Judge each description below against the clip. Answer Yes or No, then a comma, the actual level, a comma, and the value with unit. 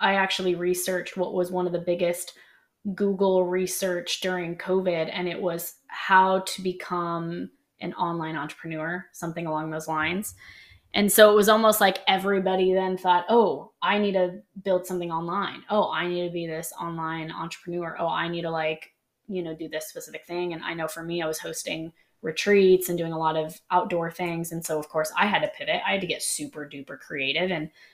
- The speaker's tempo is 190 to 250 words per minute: Yes, average, 200 wpm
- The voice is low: No, medium, 175 Hz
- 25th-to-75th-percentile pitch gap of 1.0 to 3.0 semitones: Yes, narrow, 2.5 semitones